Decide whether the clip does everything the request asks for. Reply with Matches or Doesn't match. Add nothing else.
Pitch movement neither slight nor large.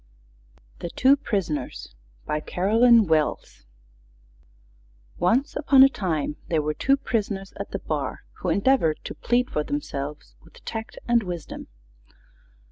Doesn't match